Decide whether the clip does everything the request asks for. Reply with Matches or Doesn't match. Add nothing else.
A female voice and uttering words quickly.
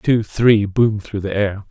Doesn't match